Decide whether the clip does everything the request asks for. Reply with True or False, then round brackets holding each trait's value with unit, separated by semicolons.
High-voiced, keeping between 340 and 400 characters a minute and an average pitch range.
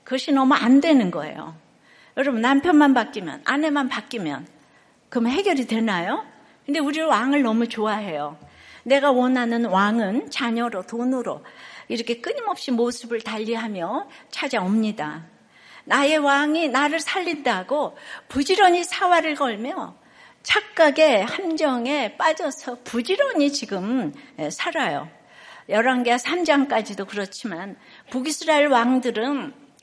False (265 Hz; 270 characters per minute; 4.6 semitones)